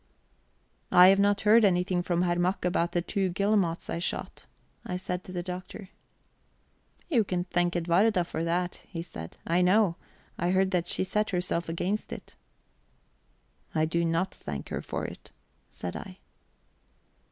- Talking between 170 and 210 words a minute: No, average, 160 wpm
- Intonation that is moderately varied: No, narrow, 1.9 semitones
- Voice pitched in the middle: Yes, medium, 180 Hz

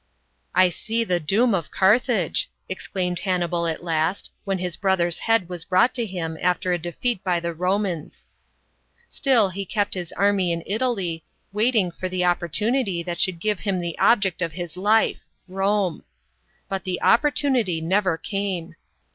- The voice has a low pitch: No, medium, 185 Hz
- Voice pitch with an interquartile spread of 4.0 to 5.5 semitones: No, average, 3.0 semitones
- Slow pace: No, average, 160 wpm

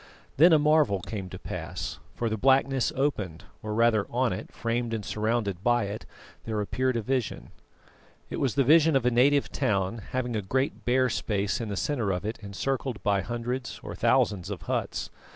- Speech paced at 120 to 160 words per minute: No, average, 190 wpm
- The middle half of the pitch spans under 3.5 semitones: No, average, 4.2 semitones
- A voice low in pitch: Yes, low, 115 Hz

